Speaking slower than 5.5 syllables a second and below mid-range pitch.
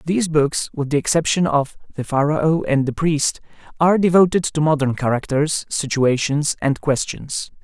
No: 4.8 syllables/s; medium, 150 Hz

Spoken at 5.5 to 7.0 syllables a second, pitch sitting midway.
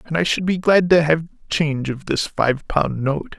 No: 4.5 syllables/s; medium, 155 Hz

